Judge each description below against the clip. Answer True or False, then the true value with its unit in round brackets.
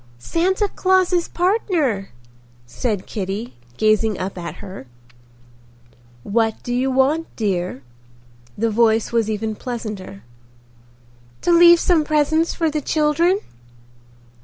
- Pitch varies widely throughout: True (7.9 semitones)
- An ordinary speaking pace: False (110 wpm)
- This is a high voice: True (240 Hz)